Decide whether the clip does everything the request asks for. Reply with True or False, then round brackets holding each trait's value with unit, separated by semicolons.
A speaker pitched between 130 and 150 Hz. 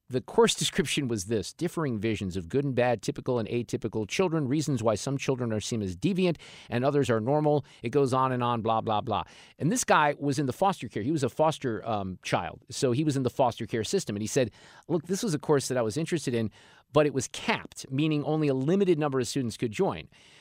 True (135 Hz)